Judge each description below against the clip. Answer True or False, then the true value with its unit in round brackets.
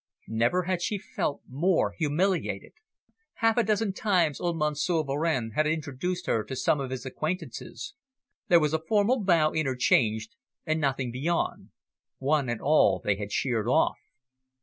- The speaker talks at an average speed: True (155 wpm)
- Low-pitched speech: False (155 Hz)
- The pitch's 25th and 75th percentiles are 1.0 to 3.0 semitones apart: False (5.3 semitones)